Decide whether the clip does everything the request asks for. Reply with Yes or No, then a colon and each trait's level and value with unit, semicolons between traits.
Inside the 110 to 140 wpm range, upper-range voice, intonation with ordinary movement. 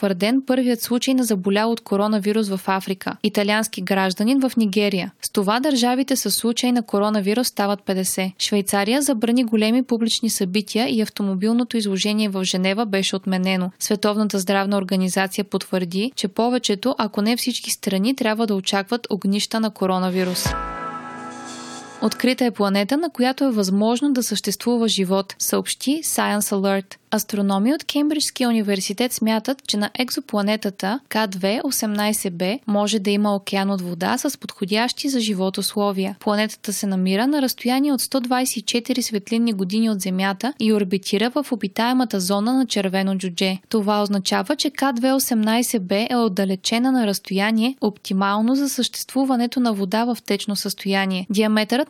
Yes: average, 135 wpm; high, 215 Hz; average, 3.4 semitones